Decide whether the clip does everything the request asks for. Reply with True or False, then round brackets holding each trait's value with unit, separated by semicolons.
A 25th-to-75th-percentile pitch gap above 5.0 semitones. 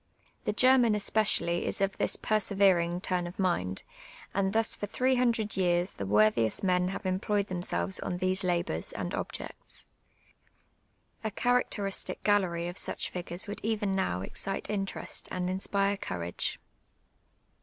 False (2.8 semitones)